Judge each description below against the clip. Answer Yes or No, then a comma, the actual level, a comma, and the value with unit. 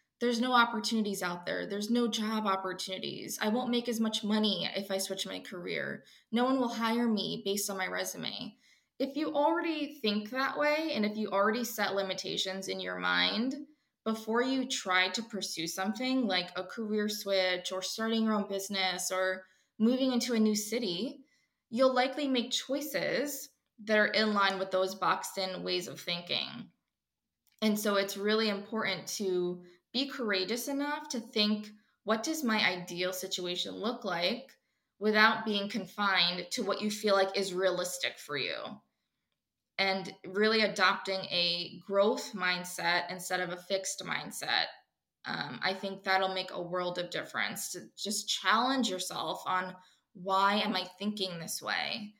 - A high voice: Yes, high, 205 Hz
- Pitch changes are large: No, average, 3.8 semitones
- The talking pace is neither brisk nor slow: Yes, average, 160 wpm